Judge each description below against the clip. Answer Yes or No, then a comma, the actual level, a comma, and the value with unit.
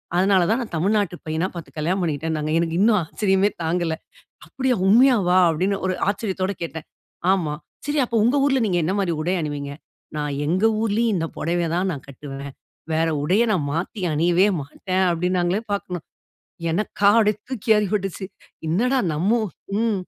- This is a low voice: No, medium, 185 Hz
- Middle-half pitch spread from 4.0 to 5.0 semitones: Yes, average, 4.3 semitones